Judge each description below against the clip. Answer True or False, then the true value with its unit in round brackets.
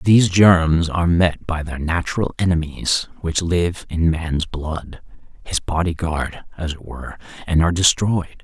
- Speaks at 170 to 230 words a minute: False (140 wpm)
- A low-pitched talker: True (85 Hz)